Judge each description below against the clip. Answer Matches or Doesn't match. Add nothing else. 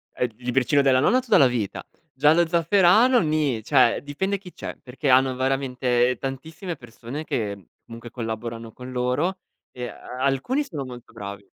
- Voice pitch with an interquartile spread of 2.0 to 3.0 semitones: Doesn't match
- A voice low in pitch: Matches